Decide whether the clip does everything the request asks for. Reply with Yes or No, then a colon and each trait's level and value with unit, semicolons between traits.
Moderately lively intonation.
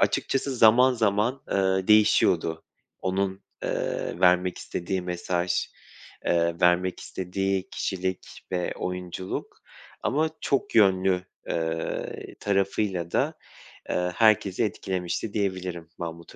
No: narrow, 2.3 semitones